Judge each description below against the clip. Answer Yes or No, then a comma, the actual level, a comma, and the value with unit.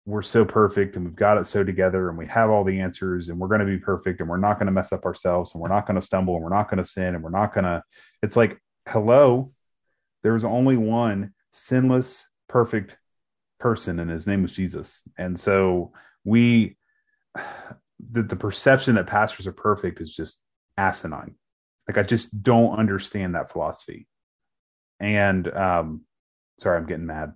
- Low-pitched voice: Yes, low, 100 Hz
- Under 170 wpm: No, average, 190 wpm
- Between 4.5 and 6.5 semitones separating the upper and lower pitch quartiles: No, average, 3.5 semitones